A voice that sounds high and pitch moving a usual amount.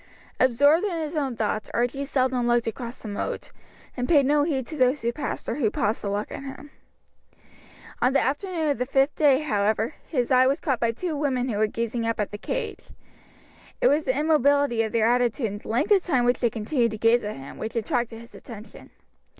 Yes: very high, 250 Hz; average, 4.0 semitones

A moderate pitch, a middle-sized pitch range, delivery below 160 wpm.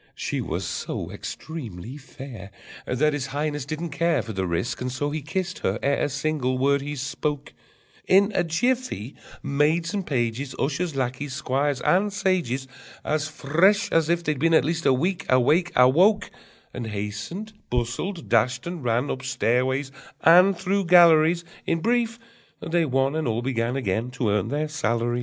No: medium, 145 Hz; average, 5.0 semitones; average, 165 wpm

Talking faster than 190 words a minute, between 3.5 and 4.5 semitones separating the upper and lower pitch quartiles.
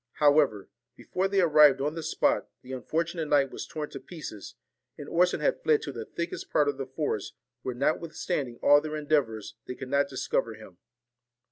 No: average, 180 wpm; average, 3.9 semitones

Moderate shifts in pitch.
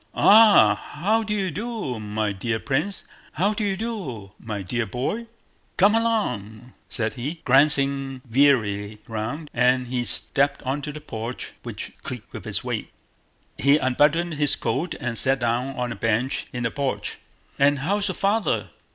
No: wide, 6.8 semitones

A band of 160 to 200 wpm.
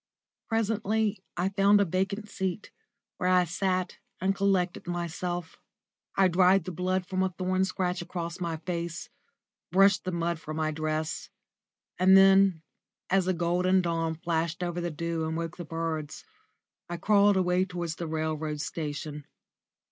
No: average, 150 wpm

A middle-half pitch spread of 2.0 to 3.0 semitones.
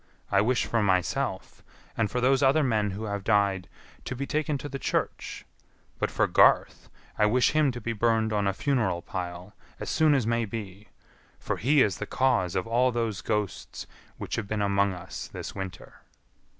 No: average, 4.2 semitones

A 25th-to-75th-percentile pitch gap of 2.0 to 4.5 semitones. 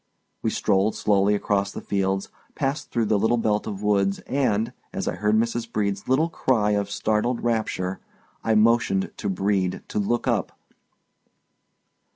Yes: average, 2.7 semitones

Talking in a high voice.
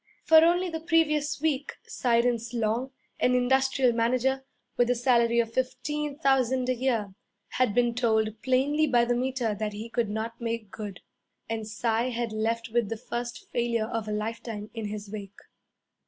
Yes: high, 235 Hz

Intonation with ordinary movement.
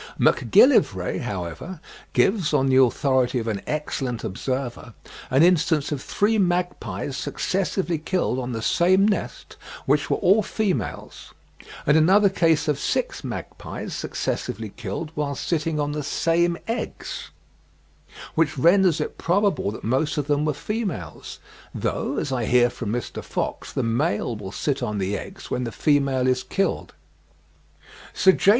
No: wide, 6.0 semitones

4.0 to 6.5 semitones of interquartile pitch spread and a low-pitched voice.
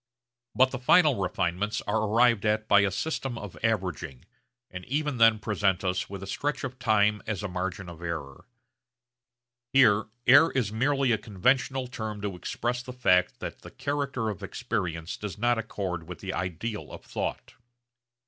Yes: average, 4.7 semitones; low, 105 Hz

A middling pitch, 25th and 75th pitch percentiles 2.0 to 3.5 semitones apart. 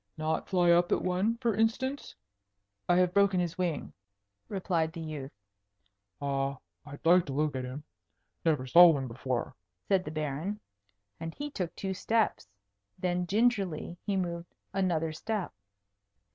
No: medium, 175 Hz; average, 4.0 semitones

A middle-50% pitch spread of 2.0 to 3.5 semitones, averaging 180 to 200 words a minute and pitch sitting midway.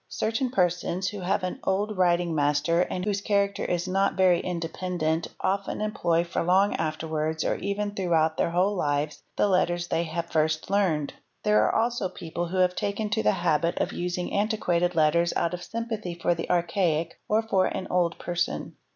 Yes: average, 3.0 semitones; average, 185 wpm; medium, 180 Hz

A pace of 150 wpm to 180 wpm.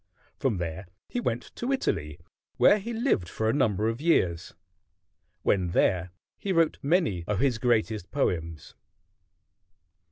No: slow, 135 wpm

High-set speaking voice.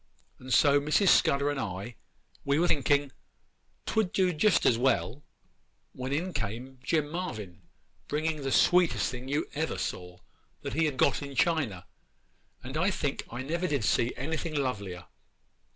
No: medium, 140 Hz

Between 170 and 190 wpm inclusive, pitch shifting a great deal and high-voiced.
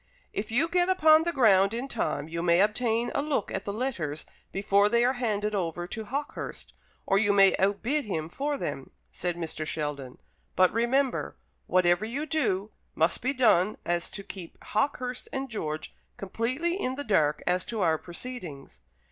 Yes: average, 175 wpm; wide, 6.5 semitones; high, 210 Hz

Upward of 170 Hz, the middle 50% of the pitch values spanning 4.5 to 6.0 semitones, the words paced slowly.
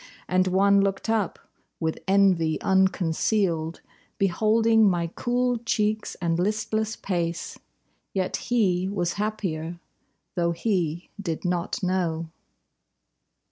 No: high, 190 Hz; average, 3.9 semitones; slow, 100 wpm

